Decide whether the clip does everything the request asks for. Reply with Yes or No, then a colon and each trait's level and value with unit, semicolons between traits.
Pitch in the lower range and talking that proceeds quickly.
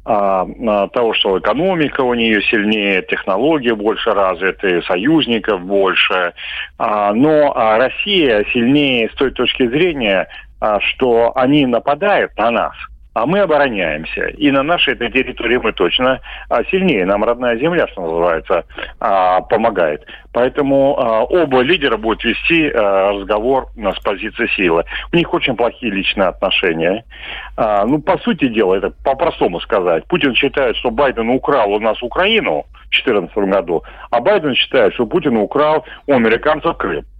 No: low, 130 Hz; average, 130 wpm